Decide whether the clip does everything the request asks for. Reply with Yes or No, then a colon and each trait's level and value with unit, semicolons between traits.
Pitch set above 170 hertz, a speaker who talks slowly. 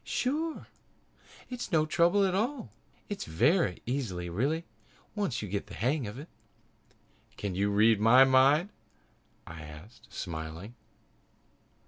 No: low, 125 Hz; slow, 125 wpm